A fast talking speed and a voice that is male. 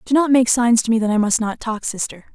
No: fast, 305 wpm; female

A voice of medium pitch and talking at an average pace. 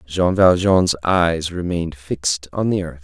No: very low, 85 Hz; average, 160 wpm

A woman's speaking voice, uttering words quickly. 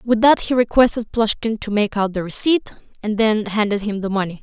Yes: female; fast, 215 wpm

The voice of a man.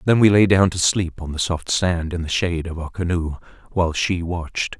Yes: male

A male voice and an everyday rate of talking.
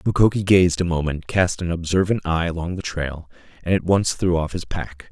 No: male; fast, 210 wpm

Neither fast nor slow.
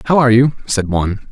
No: fast, 230 wpm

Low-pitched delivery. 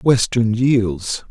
Yes: low, 115 Hz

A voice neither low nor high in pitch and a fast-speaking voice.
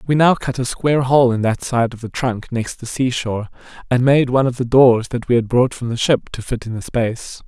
No: low, 125 Hz; fast, 275 wpm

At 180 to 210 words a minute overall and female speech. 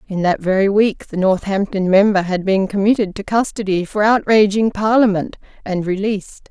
No: average, 155 wpm; female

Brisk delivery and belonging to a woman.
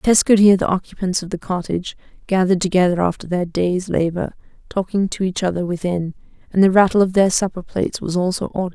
No: average, 185 wpm; female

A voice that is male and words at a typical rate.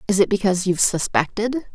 No: female; average, 170 wpm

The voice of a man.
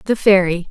No: female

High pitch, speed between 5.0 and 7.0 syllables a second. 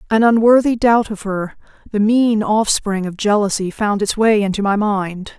No: high, 210 Hz; 4.6 syllables/s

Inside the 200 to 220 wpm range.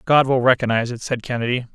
Yes: fast, 205 wpm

